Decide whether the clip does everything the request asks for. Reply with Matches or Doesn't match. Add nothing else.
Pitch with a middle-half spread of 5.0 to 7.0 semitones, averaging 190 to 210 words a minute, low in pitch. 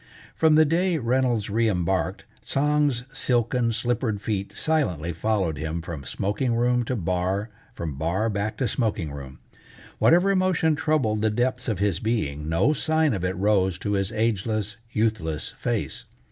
Doesn't match